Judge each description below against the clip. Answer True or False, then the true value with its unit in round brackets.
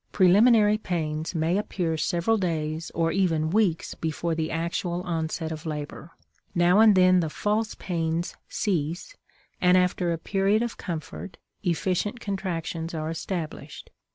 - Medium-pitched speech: True (175 Hz)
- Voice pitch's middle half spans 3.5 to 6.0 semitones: False (3.1 semitones)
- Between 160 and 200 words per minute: False (135 wpm)